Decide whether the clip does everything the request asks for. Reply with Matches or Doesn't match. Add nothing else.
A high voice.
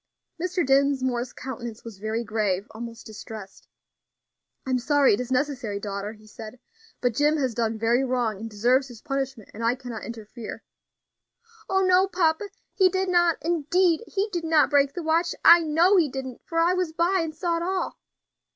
Matches